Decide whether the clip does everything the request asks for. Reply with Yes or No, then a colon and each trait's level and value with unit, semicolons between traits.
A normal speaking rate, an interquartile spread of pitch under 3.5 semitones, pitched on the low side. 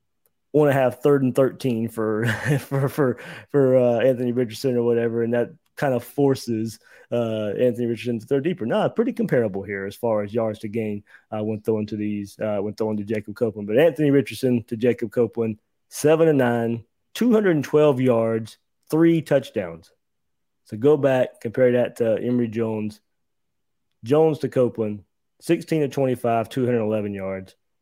No: average, 175 wpm; average, 3.8 semitones; low, 120 Hz